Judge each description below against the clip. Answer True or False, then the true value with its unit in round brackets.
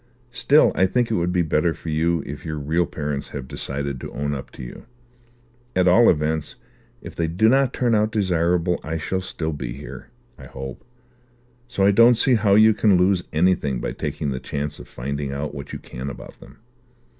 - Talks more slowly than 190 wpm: False (200 wpm)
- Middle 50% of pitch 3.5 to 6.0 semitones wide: True (5.4 semitones)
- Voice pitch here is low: True (80 Hz)